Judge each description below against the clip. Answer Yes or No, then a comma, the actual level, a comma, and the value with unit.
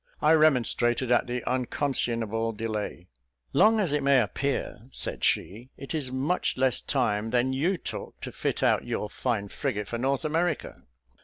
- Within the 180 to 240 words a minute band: No, average, 160 wpm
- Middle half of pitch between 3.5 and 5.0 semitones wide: Yes, average, 4.1 semitones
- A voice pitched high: No, low, 130 Hz